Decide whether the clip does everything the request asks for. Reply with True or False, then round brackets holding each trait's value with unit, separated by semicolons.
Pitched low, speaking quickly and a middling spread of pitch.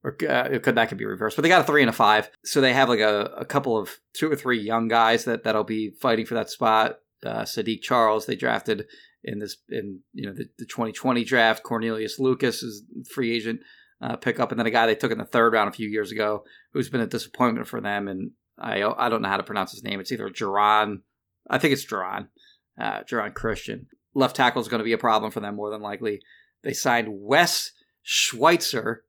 False (110 Hz; 235 wpm; 1.6 semitones)